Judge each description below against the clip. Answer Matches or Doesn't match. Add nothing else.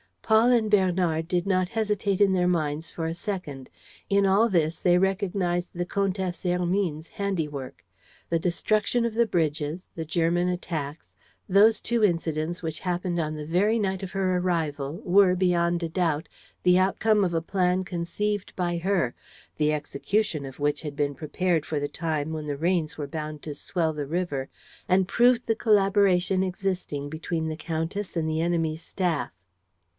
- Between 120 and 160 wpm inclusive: Doesn't match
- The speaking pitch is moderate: Matches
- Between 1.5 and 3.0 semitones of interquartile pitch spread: Doesn't match